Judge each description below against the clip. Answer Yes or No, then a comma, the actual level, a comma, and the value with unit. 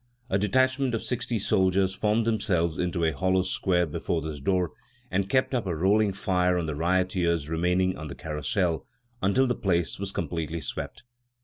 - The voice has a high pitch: No, very low, 95 Hz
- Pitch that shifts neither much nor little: Yes, average, 3.1 semitones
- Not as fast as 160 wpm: No, average, 175 wpm